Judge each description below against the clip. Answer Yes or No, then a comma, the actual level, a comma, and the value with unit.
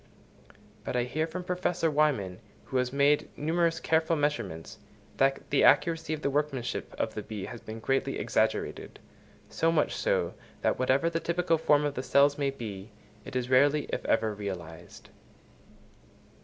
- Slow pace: No, average, 160 wpm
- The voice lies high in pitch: No, medium, 140 Hz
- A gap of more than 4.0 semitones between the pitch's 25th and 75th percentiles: Yes, average, 5.2 semitones